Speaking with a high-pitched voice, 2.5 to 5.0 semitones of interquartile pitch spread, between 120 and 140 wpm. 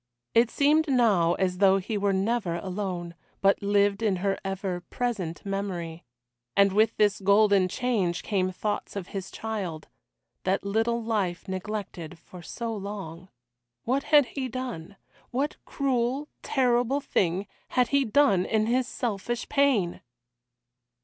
Yes: high, 205 Hz; average, 4.4 semitones; slow, 135 wpm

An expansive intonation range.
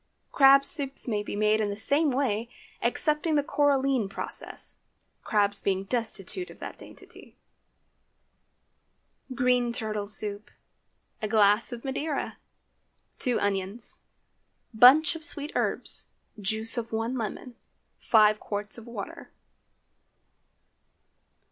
No: average, 4.5 semitones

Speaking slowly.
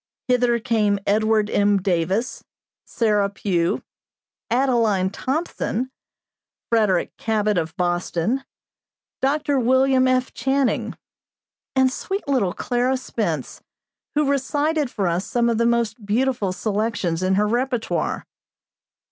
Yes: slow, 110 wpm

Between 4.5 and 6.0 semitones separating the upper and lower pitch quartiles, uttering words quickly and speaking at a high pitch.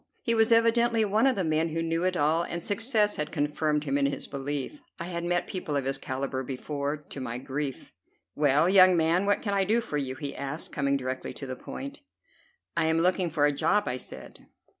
No: wide, 5.6 semitones; fast, 220 wpm; medium, 160 Hz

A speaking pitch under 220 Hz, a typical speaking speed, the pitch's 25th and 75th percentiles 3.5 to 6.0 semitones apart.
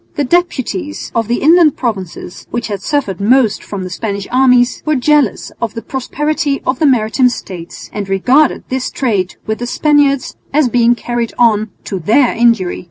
No: high, 245 Hz; average, 170 wpm; average, 4.7 semitones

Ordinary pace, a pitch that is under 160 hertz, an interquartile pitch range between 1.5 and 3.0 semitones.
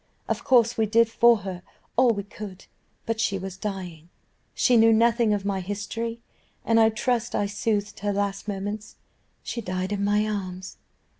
No: average, 170 wpm; high, 205 Hz; narrow, 2.6 semitones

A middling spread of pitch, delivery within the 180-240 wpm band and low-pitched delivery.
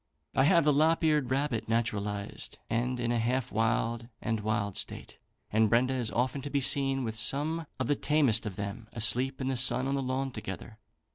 Yes: average, 3.5 semitones; average, 200 wpm; low, 125 Hz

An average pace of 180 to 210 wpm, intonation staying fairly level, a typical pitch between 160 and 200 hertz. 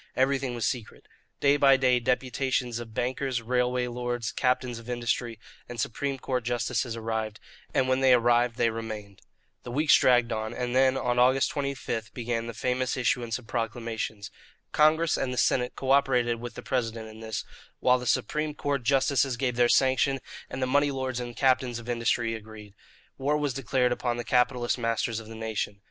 No: average, 185 wpm; narrow, 2.3 semitones; low, 125 Hz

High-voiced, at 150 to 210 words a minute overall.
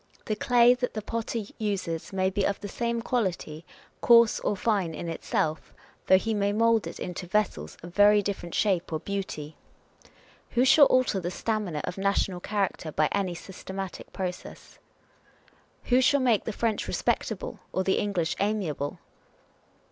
Yes: high, 200 Hz; average, 160 wpm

